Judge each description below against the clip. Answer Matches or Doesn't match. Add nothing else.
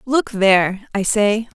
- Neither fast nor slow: Matches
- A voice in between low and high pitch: Doesn't match